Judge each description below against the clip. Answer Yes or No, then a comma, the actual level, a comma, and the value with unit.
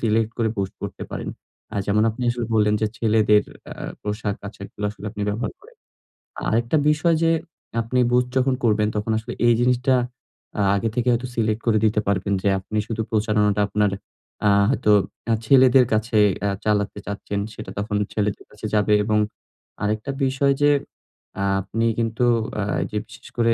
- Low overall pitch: Yes, low, 110 Hz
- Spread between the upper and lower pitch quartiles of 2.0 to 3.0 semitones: Yes, narrow, 2.5 semitones